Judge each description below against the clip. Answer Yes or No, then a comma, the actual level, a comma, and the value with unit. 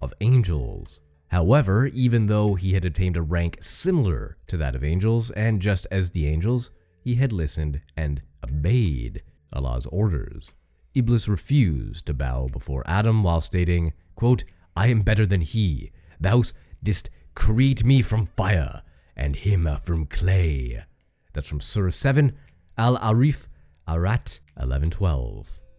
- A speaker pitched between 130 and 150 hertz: No, very low, 90 Hz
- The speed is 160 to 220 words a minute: No, slow, 135 wpm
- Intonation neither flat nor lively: No, wide, 6.7 semitones